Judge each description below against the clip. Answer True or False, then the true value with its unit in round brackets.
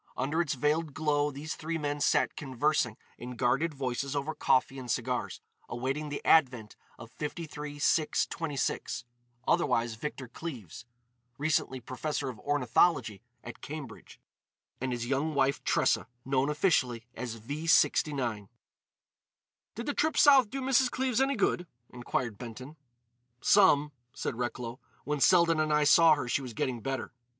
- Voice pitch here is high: False (140 Hz)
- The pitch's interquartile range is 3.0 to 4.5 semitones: True (3.9 semitones)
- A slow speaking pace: False (145 wpm)